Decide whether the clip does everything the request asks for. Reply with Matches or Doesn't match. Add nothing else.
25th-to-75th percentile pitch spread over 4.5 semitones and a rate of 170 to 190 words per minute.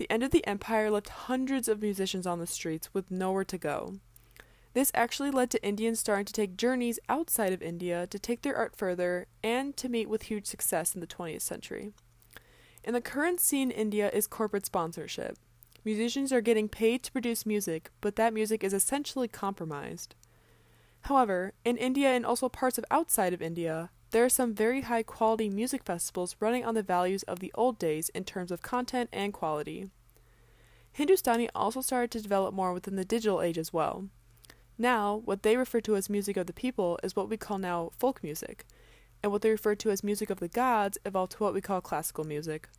Doesn't match